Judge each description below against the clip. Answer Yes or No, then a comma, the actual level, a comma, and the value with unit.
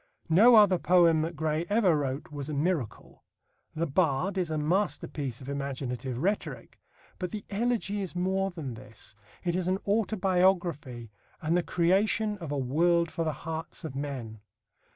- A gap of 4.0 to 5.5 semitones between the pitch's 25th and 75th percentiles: Yes, average, 5.0 semitones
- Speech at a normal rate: Yes, average, 160 wpm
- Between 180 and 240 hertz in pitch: No, medium, 165 Hz